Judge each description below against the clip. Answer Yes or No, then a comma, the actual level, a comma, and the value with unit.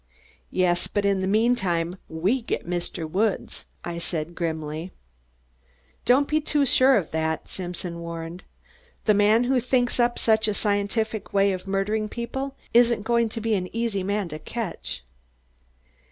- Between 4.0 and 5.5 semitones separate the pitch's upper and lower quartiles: Yes, average, 5.0 semitones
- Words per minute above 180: No, average, 155 wpm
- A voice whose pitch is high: Yes, high, 200 Hz